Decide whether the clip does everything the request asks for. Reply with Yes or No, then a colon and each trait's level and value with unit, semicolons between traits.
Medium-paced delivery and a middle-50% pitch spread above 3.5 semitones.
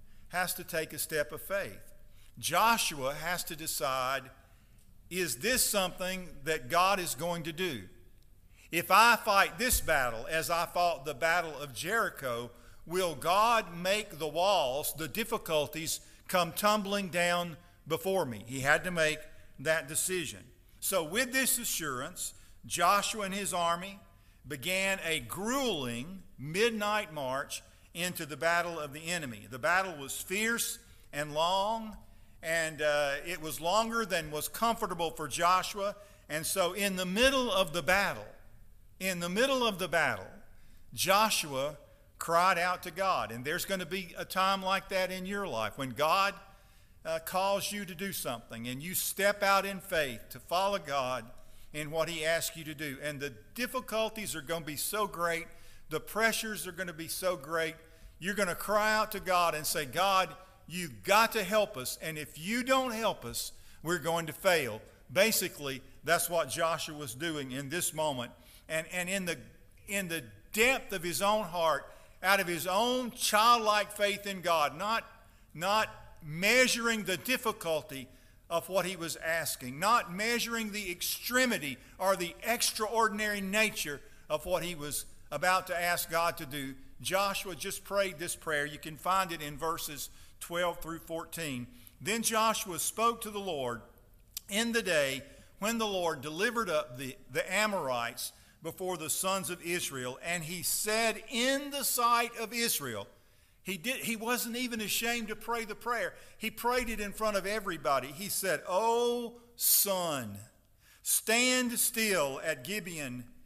Yes: average, 160 wpm; wide, 5.6 semitones